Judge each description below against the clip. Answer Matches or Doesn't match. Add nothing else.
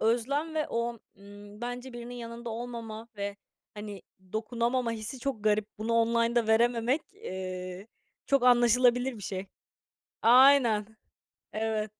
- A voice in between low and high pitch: Doesn't match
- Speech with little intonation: Matches